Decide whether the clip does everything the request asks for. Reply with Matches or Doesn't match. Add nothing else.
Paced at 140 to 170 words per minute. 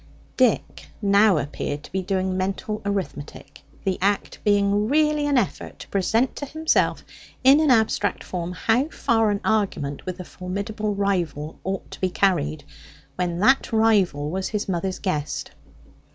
Matches